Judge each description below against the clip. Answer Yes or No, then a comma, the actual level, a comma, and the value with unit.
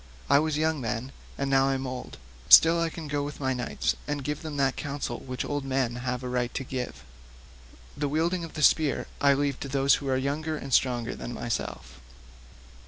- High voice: No, low, 135 Hz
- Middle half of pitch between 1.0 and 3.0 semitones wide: Yes, narrow, 2.6 semitones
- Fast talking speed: Yes, fast, 210 wpm